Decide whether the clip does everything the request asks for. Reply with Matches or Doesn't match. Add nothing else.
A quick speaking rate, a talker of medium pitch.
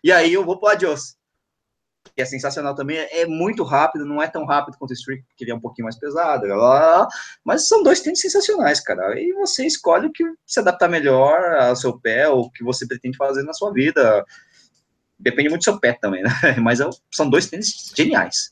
Matches